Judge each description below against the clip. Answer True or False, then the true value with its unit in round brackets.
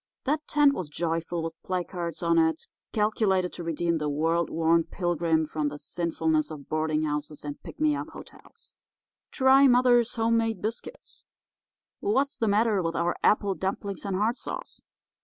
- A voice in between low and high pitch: True (175 Hz)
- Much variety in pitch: True (5.8 semitones)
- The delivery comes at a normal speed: True (160 wpm)